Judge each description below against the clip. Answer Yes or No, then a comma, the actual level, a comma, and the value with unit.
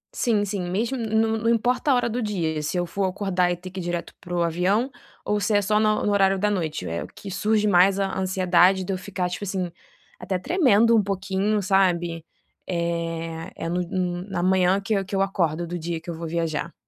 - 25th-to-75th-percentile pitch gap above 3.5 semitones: No, average, 3.0 semitones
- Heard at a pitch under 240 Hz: Yes, high, 190 Hz